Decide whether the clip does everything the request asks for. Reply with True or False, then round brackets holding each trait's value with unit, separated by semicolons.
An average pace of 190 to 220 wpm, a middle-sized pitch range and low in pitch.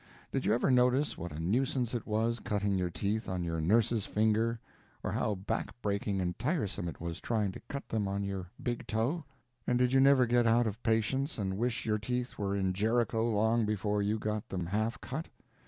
True (205 wpm; 3.3 semitones; 110 Hz)